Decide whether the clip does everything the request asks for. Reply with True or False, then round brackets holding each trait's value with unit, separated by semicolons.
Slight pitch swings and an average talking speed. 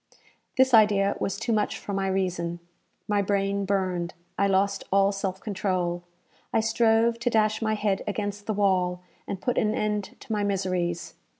True (2.1 semitones; 170 wpm)